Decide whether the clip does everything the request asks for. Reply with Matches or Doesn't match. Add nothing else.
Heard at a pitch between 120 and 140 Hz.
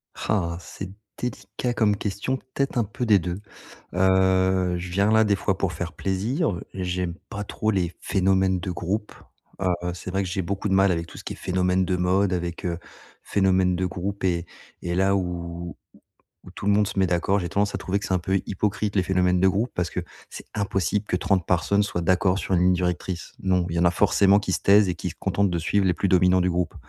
Doesn't match